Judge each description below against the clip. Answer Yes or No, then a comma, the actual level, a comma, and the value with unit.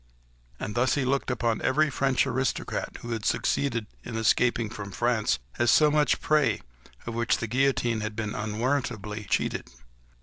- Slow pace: No, average, 160 wpm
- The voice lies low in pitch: Yes, low, 120 Hz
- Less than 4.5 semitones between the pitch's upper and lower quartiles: Yes, average, 3.2 semitones